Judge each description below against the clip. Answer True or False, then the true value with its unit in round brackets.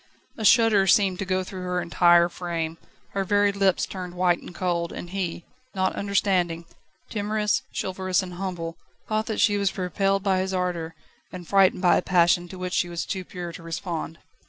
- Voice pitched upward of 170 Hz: True (185 Hz)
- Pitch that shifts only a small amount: True (2.1 semitones)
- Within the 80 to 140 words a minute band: False (185 wpm)